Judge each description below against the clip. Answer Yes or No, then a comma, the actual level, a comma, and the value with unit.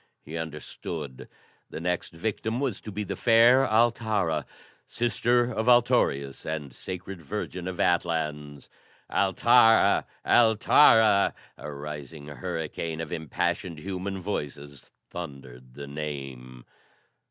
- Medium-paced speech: No, slow, 110 wpm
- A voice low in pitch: Yes, very low, 85 Hz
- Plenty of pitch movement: Yes, wide, 6.6 semitones